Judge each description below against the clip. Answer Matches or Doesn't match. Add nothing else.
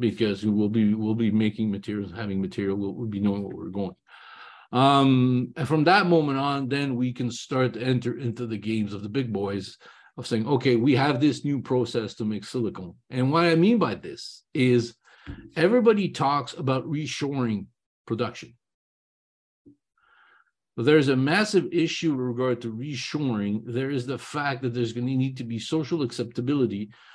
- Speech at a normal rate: Matches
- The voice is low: Matches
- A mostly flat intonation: Doesn't match